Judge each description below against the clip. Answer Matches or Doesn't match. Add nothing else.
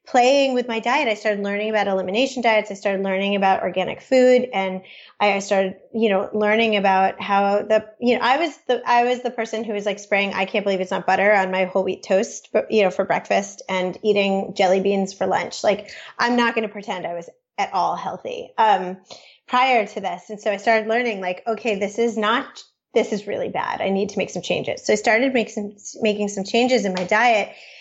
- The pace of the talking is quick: Matches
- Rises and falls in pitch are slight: Doesn't match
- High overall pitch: Matches